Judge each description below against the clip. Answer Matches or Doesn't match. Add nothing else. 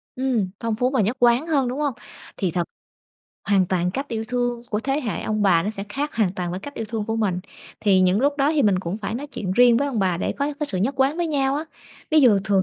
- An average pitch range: Doesn't match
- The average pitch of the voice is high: Matches